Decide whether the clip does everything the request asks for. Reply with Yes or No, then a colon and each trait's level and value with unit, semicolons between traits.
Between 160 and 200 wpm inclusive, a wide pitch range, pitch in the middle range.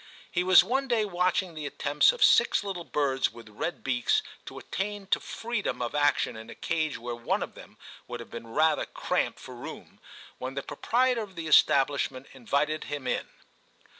Yes: average, 190 wpm; wide, 6.6 semitones; medium, 150 Hz